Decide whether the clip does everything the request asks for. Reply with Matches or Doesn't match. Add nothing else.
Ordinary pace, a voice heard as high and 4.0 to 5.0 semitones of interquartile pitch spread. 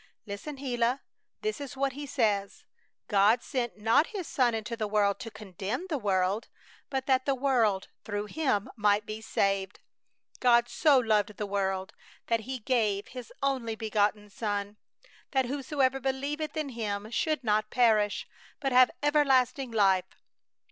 Matches